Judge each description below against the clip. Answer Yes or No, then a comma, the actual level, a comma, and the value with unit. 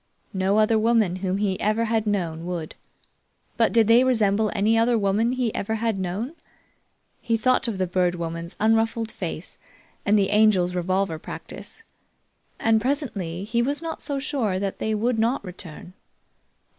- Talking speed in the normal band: Yes, average, 160 wpm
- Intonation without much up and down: No, average, 3.5 semitones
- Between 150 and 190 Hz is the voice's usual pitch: No, high, 215 Hz